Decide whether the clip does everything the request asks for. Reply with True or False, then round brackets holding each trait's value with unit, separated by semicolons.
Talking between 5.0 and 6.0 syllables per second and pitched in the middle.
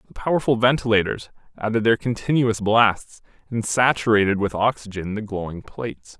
False (5.3 syllables/s; 110 Hz)